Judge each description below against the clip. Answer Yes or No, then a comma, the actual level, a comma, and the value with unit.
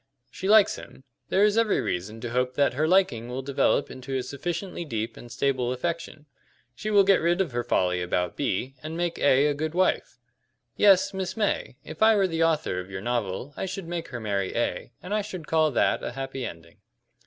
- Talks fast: Yes, fast, 210 wpm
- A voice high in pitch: No, medium, 145 Hz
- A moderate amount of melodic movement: No, wide, 7.1 semitones